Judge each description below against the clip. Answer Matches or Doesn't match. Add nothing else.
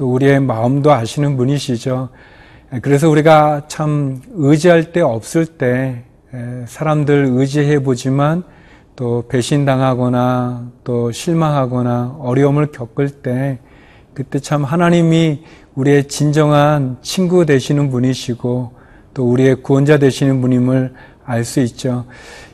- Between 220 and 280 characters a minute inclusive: Matches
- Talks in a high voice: Doesn't match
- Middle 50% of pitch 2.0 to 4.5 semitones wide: Matches